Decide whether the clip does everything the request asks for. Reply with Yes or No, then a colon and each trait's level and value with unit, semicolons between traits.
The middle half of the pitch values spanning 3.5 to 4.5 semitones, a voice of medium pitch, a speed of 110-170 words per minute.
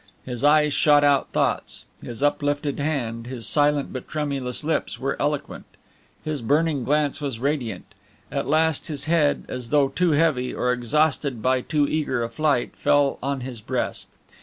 No: average, 3.0 semitones; medium, 145 Hz; average, 160 wpm